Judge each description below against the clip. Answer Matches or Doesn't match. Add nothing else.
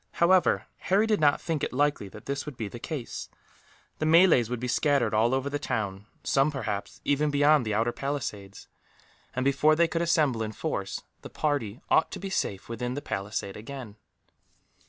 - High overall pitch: Doesn't match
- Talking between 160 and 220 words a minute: Matches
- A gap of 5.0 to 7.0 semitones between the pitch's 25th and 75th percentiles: Matches